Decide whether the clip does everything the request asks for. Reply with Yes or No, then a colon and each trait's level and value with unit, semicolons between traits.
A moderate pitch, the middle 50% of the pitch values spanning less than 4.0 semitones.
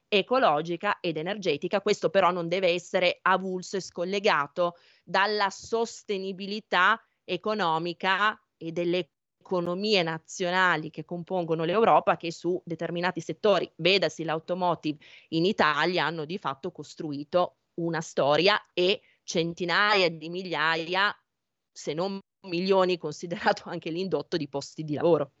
Yes: medium, 175 Hz; average, 2.8 semitones